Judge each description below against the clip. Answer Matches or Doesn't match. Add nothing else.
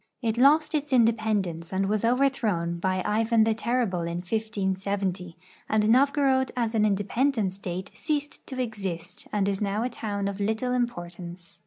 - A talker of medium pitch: Doesn't match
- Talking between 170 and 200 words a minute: Doesn't match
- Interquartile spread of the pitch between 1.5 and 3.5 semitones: Doesn't match